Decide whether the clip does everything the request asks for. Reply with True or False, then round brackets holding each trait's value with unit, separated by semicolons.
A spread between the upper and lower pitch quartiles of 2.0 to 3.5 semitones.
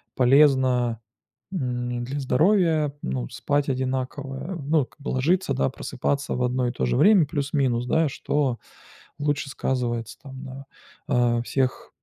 True (2.8 semitones)